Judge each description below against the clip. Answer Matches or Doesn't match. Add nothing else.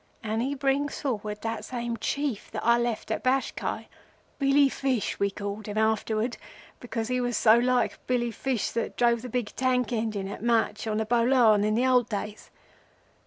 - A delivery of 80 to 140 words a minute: Doesn't match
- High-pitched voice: Matches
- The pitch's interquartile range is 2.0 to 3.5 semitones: Matches